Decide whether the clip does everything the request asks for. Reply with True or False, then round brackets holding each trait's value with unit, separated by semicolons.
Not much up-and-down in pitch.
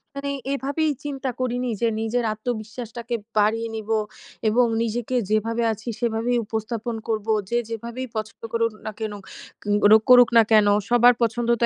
True (2.0 semitones)